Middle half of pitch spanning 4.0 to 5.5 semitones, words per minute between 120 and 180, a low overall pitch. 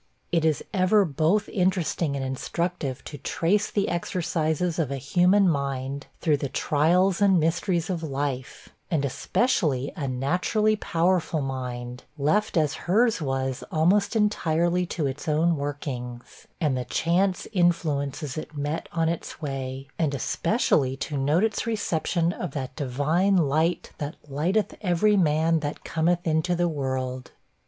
No: average, 4.3 semitones; average, 145 wpm; medium, 160 Hz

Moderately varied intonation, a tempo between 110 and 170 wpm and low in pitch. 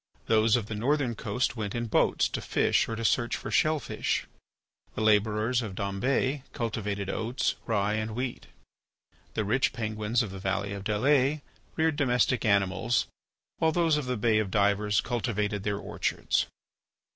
Yes: average, 3.3 semitones; average, 160 wpm; low, 110 Hz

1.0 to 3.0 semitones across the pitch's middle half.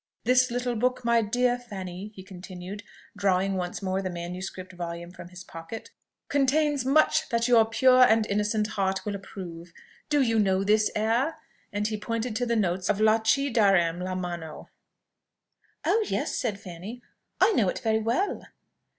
No: average, 4.5 semitones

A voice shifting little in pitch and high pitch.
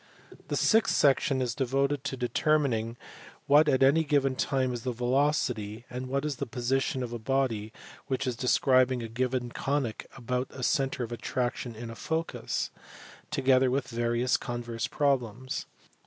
No: narrow, 2.3 semitones; low, 130 Hz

